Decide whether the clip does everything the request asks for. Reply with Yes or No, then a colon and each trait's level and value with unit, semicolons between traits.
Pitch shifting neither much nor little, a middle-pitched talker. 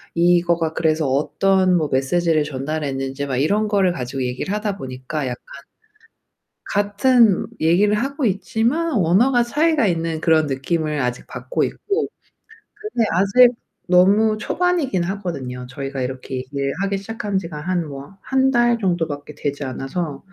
No: wide, 6.8 semitones; medium, 175 Hz